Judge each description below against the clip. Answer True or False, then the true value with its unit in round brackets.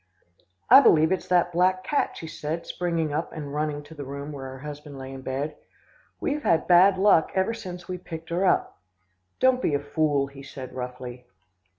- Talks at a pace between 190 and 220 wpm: True (195 wpm)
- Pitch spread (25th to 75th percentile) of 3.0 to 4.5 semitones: True (4.1 semitones)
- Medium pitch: True (155 Hz)